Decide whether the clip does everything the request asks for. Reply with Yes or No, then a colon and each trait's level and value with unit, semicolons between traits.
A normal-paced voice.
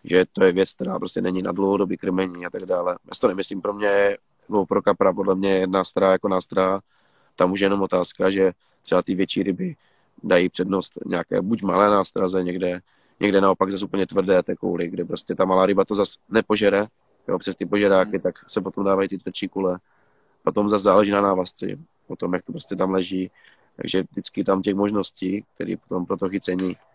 No: fast, 205 wpm